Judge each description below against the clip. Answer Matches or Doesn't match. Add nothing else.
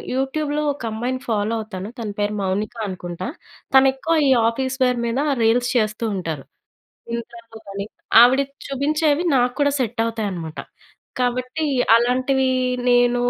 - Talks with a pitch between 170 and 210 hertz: Doesn't match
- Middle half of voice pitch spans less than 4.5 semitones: Matches